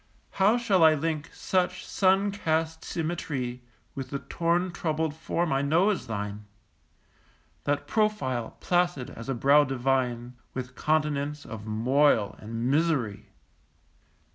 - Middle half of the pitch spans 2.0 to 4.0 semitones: No, average, 5.2 semitones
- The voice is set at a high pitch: No, medium, 150 Hz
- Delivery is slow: Yes, slow, 125 wpm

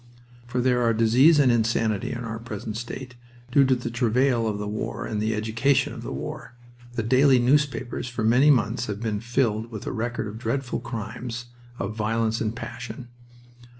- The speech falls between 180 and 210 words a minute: Yes, average, 185 wpm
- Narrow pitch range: Yes, narrow, 2.2 semitones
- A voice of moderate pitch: No, low, 115 Hz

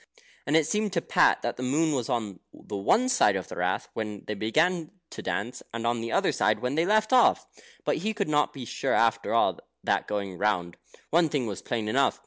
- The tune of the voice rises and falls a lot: Yes, wide, 7.2 semitones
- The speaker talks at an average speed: No, fast, 225 wpm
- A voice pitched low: Yes, low, 120 Hz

